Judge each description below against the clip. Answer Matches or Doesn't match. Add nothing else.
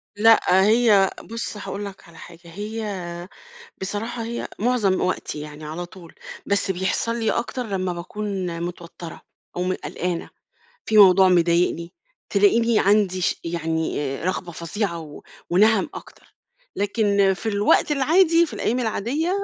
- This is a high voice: Matches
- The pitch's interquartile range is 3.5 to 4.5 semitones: Matches